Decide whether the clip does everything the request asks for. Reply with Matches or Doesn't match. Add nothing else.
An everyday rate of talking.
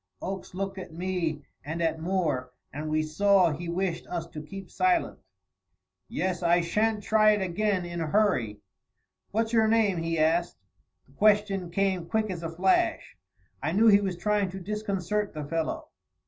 Matches